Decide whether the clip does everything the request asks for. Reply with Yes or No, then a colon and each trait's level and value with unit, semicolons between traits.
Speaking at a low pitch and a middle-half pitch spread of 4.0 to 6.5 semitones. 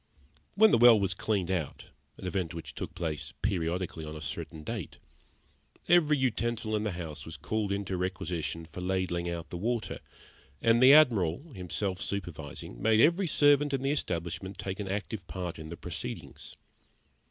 Yes: very low, 95 Hz; average, 5.2 semitones